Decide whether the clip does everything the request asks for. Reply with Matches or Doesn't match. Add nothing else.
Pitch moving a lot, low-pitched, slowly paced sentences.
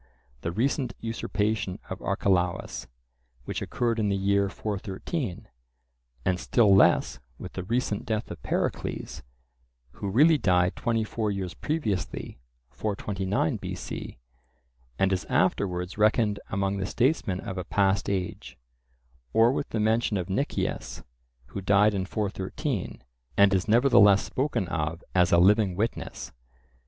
Doesn't match